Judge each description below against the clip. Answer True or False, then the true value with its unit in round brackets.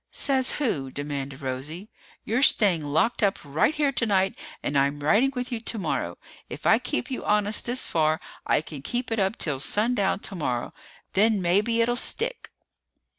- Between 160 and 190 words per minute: True (165 wpm)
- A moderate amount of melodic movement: False (8.2 semitones)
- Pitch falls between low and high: False (195 Hz)